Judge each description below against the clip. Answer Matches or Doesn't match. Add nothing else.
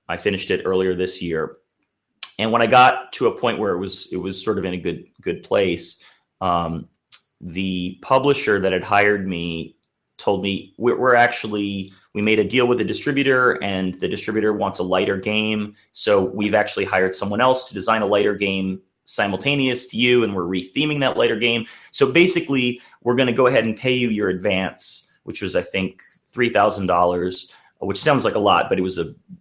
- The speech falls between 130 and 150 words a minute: Doesn't match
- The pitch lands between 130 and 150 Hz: Doesn't match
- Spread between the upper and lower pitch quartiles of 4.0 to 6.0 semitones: Matches